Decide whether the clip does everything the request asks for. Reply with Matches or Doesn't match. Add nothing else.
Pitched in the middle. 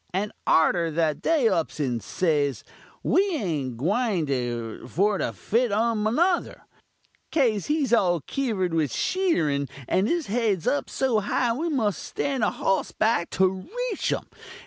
Doesn't match